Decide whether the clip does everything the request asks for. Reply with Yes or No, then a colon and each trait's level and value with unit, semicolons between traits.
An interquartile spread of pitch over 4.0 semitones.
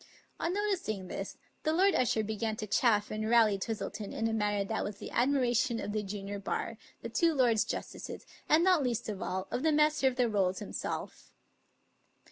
Yes: average, 4.4 semitones